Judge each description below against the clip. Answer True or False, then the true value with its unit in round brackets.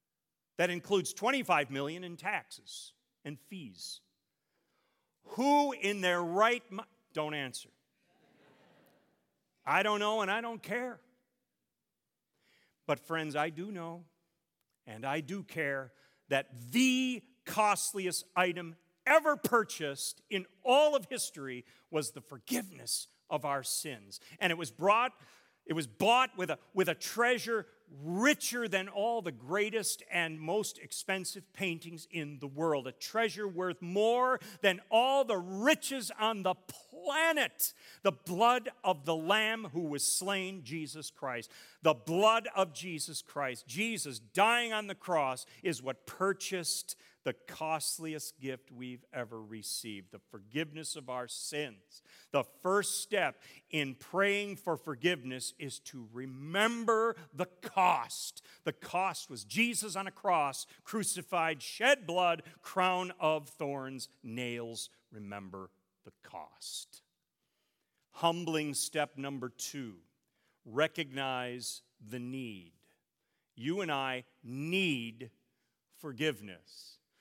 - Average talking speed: False (125 wpm)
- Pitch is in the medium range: True (170 Hz)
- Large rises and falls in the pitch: True (6.7 semitones)